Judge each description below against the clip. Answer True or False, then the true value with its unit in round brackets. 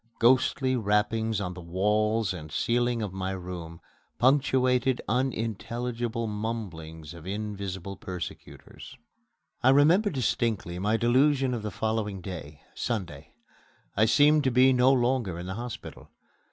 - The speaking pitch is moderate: False (110 Hz)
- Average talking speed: False (125 wpm)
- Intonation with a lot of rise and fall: False (4.8 semitones)